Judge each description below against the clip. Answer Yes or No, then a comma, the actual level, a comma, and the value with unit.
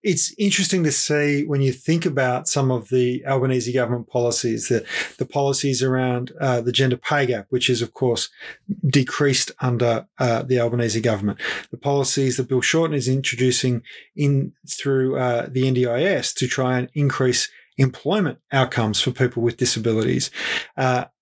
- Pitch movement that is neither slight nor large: No, narrow, 2.2 semitones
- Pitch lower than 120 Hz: No, low, 130 Hz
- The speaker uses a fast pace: No, average, 160 wpm